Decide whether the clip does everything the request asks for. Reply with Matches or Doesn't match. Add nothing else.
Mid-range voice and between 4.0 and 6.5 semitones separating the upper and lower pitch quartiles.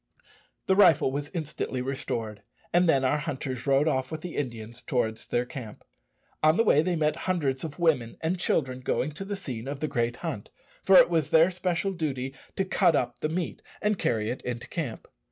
Matches